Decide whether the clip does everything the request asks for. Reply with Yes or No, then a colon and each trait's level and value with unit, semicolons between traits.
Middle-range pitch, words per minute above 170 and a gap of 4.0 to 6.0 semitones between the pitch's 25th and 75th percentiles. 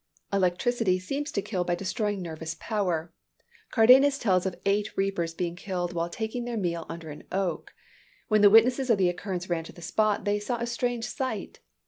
No: high, 195 Hz; average, 185 wpm; average, 4.4 semitones